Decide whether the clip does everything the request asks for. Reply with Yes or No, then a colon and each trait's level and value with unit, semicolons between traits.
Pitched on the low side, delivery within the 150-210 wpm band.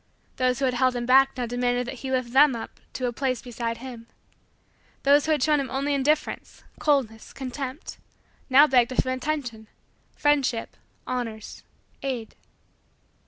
No: very high, 255 Hz; average, 160 wpm